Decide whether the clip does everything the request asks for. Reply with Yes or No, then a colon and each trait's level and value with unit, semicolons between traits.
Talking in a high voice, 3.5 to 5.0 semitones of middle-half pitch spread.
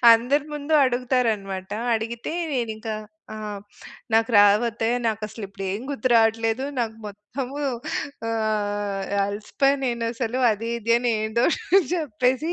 No: high, 225 Hz; average, 2.8 semitones